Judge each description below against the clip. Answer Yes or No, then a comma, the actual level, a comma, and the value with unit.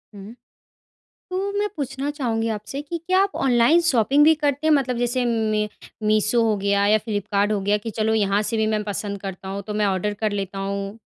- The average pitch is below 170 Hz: No, high, 220 Hz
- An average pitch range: Yes, average, 4.7 semitones